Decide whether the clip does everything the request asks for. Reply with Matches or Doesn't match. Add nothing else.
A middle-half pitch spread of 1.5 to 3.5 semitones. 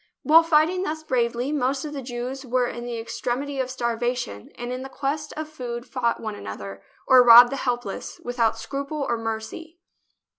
Matches